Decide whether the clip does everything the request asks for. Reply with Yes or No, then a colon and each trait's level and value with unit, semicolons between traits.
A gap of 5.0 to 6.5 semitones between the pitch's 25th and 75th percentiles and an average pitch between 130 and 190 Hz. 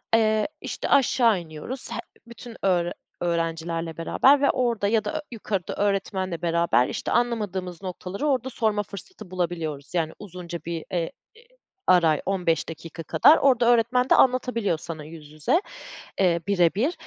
Yes: wide, 5.5 semitones; medium, 185 Hz